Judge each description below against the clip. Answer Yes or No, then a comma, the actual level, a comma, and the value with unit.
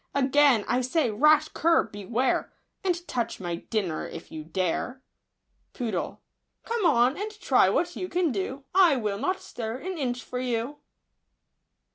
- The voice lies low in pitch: No, very high, 255 Hz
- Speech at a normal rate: Yes, average, 150 wpm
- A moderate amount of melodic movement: No, wide, 6.1 semitones